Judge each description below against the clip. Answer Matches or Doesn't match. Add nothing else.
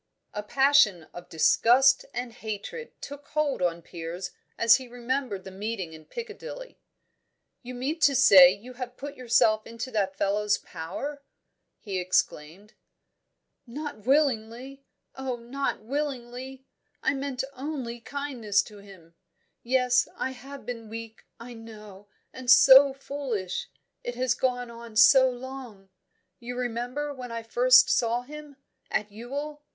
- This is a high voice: Matches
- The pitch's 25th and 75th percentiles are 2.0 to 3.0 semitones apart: Doesn't match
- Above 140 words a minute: Doesn't match